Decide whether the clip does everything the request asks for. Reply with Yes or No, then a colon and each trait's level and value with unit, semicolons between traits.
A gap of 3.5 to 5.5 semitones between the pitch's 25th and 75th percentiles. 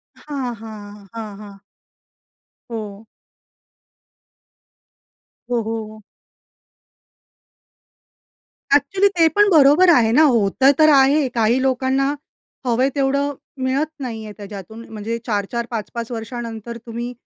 Yes: average, 3.9 semitones